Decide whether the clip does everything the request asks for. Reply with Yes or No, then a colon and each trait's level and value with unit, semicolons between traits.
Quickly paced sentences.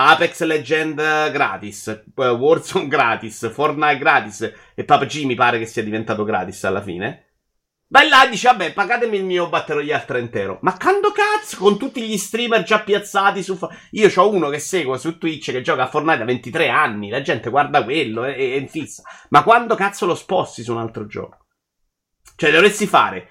Yes: fast, 180 wpm